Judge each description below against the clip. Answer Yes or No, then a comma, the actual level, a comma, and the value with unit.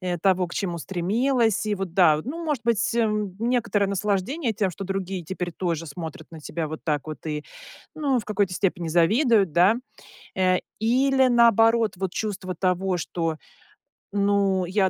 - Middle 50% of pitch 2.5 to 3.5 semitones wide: No, average, 4.3 semitones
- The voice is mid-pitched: No, high, 195 Hz